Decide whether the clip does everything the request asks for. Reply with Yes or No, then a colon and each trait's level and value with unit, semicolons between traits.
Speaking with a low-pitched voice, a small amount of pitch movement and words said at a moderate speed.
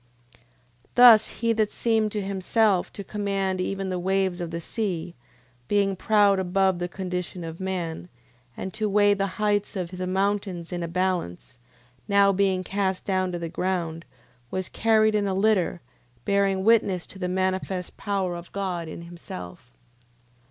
No: high, 190 Hz; narrow, 2.2 semitones; average, 165 wpm